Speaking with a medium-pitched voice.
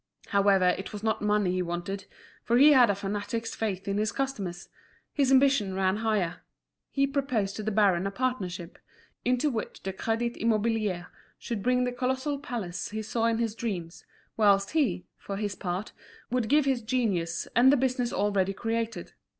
No: high, 215 Hz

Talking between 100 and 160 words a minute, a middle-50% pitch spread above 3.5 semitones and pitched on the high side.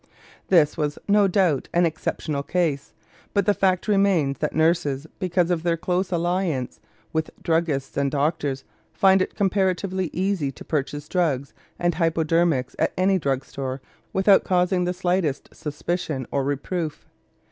No: average, 145 wpm; average, 4.0 semitones; medium, 170 Hz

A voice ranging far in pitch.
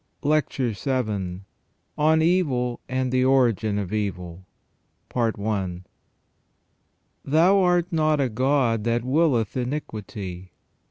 Yes: wide, 6.2 semitones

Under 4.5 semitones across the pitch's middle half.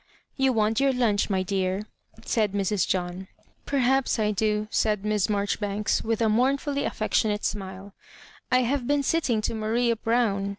Yes: average, 3.3 semitones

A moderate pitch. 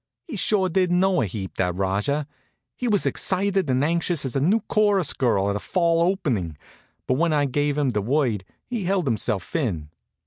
Yes: medium, 150 Hz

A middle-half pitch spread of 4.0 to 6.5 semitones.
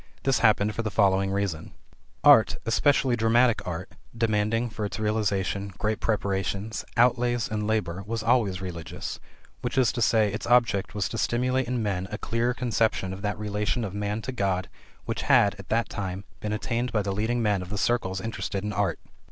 No: average, 2.8 semitones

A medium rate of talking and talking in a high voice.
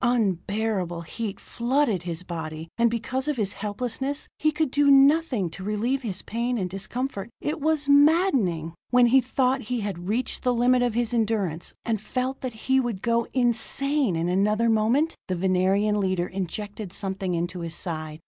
Yes: average, 170 wpm; high, 225 Hz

